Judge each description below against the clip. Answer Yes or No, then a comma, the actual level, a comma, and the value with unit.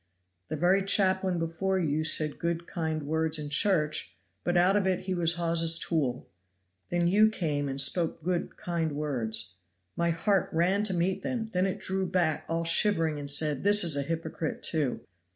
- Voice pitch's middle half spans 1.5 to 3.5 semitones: Yes, average, 3.2 semitones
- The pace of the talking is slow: No, average, 180 wpm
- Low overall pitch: No, medium, 165 Hz